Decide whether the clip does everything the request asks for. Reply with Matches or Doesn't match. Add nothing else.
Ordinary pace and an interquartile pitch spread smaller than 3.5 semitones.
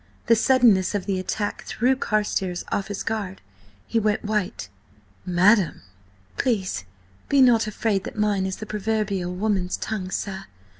Matches